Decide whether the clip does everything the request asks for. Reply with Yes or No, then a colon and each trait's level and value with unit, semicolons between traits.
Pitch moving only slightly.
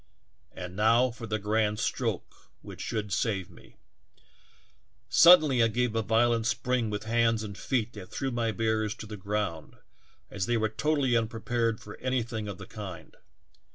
Yes: narrow, 2.1 semitones